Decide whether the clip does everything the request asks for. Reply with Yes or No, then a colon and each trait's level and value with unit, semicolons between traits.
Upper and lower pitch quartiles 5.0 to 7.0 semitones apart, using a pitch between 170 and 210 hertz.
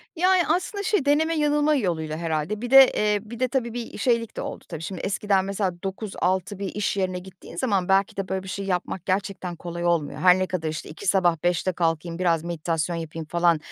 No: average, 4.1 semitones; high, 190 Hz